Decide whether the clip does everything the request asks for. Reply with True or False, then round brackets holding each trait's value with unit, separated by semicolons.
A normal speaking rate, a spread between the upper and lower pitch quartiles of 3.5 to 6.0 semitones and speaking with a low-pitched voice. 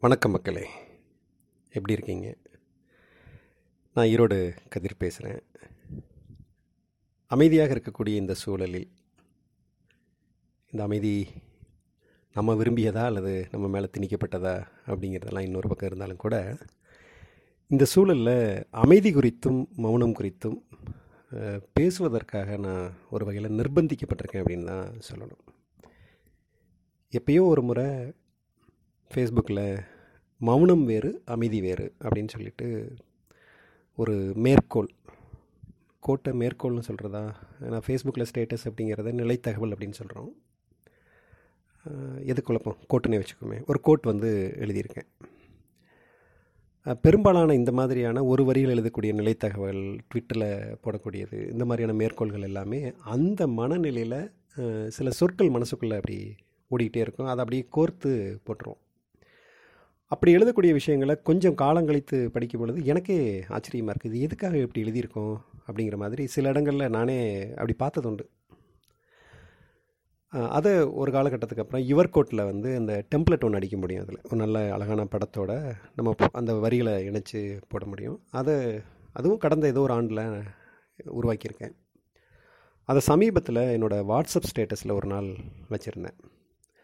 True (105 wpm; 4.3 semitones; 115 Hz)